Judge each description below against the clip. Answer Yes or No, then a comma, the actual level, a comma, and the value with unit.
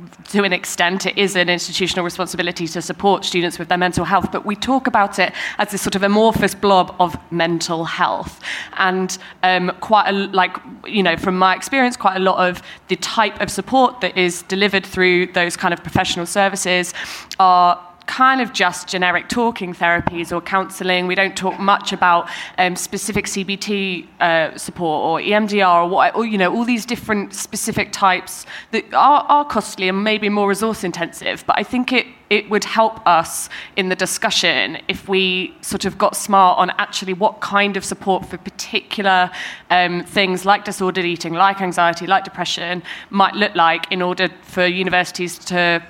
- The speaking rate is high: No, average, 180 wpm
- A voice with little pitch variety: Yes, narrow, 2.1 semitones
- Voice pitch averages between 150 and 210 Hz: Yes, medium, 185 Hz